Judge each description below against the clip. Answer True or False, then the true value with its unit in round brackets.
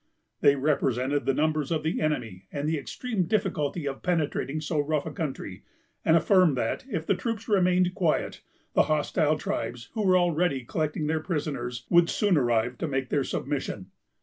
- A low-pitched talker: False (155 Hz)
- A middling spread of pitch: True (4.3 semitones)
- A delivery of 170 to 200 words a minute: True (175 wpm)